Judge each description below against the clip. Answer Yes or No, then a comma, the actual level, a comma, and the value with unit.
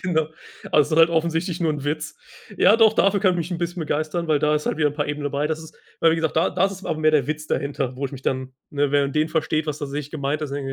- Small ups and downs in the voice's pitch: Yes, narrow, 2.2 semitones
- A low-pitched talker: No, medium, 155 Hz